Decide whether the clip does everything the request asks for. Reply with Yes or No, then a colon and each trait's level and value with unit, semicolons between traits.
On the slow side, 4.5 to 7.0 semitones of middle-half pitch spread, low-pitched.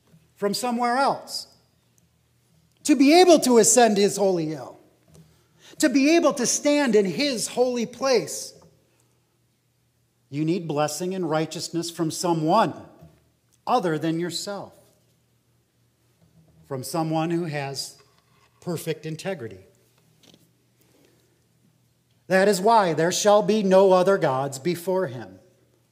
No: slow, 110 wpm; wide, 5.4 semitones; medium, 175 Hz